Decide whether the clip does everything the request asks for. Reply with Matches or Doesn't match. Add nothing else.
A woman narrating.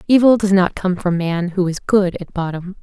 Matches